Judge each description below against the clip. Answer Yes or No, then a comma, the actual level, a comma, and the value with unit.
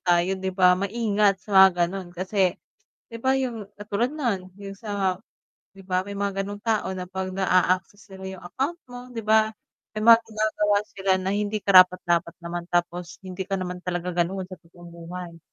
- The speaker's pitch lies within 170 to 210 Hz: Yes, high, 190 Hz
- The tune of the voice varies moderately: No, narrow, 2.3 semitones